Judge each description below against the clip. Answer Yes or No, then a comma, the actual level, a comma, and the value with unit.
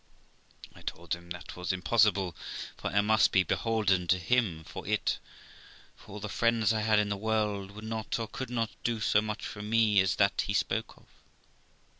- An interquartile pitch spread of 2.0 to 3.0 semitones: Yes, narrow, 2.5 semitones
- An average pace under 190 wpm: No, average, 195 wpm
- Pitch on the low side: Yes, low, 105 Hz